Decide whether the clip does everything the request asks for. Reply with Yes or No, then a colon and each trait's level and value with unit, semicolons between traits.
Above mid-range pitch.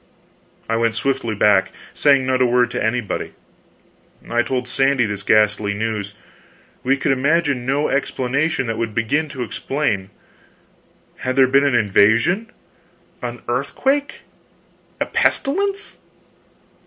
No: low, 125 Hz